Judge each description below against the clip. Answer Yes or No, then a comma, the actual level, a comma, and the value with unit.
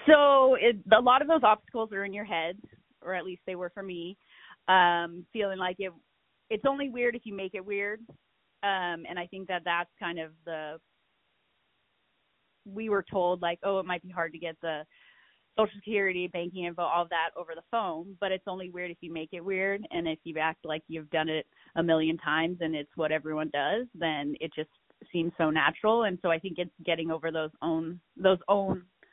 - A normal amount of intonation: Yes, average, 3.3 semitones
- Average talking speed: No, fast, 210 wpm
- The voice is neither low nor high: Yes, medium, 180 Hz